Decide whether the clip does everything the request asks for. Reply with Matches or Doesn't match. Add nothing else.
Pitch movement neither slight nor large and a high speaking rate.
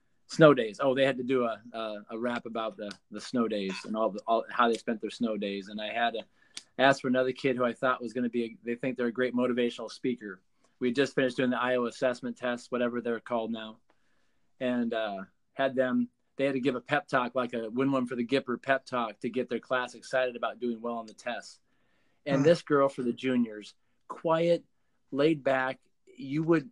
Doesn't match